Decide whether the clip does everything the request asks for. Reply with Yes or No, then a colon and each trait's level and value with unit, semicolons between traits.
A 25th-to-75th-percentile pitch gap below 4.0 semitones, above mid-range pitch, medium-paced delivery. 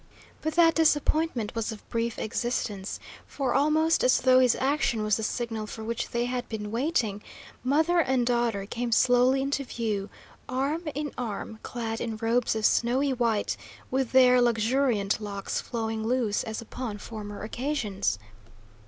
Yes: average, 3.3 semitones; high, 240 Hz; average, 155 wpm